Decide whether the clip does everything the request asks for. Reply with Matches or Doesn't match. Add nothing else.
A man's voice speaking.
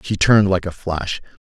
Matches